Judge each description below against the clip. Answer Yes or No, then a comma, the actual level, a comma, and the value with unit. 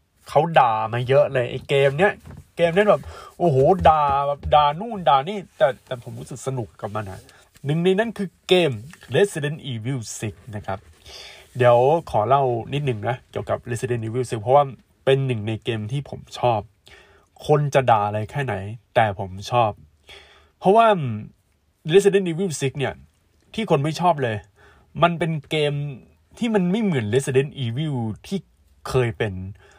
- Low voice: Yes, low, 130 Hz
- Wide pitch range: Yes, wide, 6.2 semitones